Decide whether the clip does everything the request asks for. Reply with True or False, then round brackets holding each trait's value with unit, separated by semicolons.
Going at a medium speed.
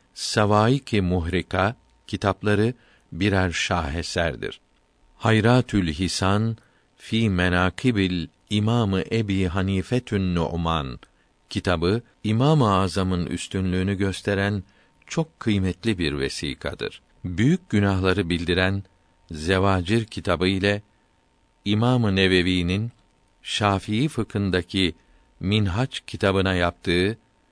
False (80 wpm)